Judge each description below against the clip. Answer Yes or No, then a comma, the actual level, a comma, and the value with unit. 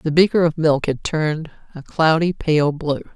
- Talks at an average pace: Yes, average, 190 wpm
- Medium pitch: Yes, medium, 155 Hz